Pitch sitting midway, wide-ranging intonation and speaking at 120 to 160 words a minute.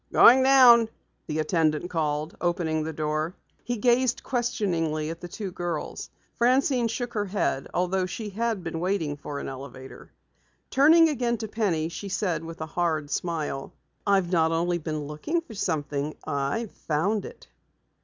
Yes: medium, 175 Hz; wide, 6.2 semitones; average, 155 wpm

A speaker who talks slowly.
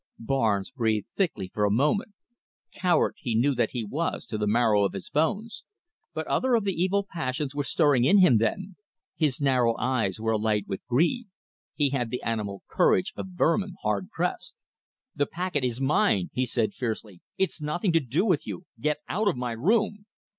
No: average, 185 wpm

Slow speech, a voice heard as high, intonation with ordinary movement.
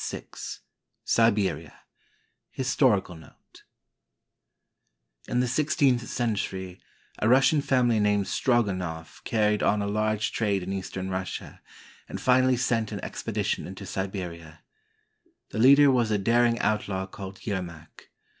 No: slow, 120 wpm; low, 105 Hz; average, 4.2 semitones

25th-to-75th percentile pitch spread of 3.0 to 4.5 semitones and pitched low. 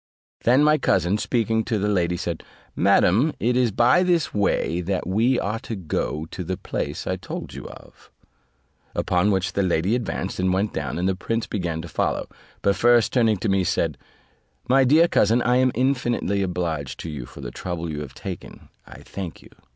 No: wide, 5.4 semitones; low, 100 Hz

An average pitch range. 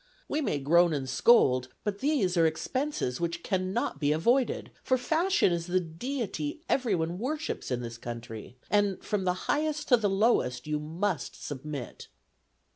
No: wide, 8.3 semitones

